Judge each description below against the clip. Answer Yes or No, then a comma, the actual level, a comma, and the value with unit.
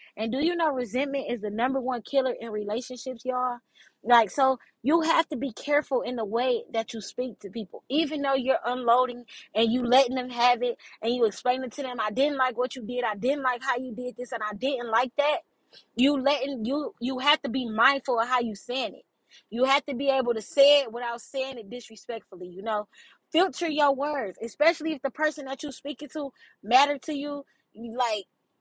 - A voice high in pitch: Yes, very high, 255 Hz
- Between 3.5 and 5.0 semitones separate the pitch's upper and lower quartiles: No, average, 3.0 semitones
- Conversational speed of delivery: No, fast, 220 wpm